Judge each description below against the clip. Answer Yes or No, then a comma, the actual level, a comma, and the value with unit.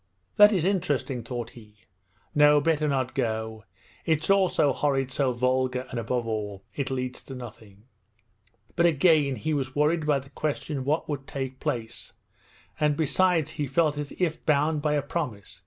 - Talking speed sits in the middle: Yes, average, 170 wpm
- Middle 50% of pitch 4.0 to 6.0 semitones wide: No, average, 3.4 semitones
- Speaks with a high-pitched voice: No, medium, 140 Hz